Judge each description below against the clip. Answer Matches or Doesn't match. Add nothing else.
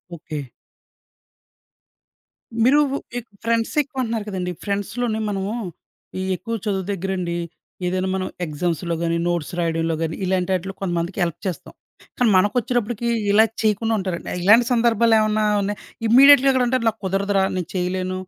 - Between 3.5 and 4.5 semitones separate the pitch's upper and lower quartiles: Matches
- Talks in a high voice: Matches